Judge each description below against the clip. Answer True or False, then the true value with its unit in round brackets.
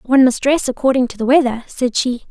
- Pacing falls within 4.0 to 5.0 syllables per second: False (6.0 syllables/s)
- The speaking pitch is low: False (255 Hz)